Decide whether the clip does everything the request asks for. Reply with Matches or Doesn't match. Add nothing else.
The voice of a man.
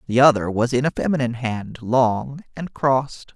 Matches